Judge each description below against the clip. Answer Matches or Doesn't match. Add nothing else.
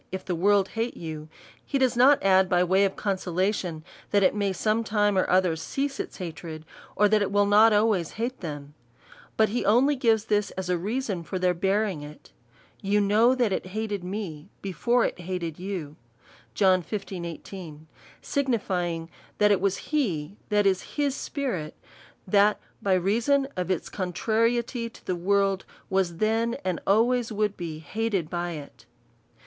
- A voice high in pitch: Matches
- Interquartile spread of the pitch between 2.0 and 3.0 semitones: Doesn't match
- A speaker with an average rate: Matches